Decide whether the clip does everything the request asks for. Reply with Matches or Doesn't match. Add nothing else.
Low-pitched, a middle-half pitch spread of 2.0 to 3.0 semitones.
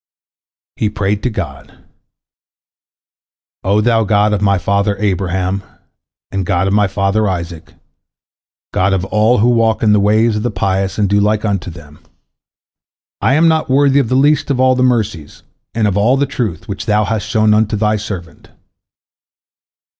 Matches